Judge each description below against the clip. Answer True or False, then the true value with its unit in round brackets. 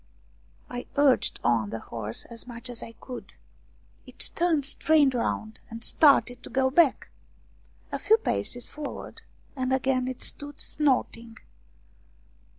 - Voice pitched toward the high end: True (255 Hz)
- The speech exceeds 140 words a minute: False (135 wpm)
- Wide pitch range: False (3.6 semitones)